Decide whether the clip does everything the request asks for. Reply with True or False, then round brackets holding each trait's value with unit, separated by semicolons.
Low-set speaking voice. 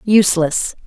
False (185 Hz)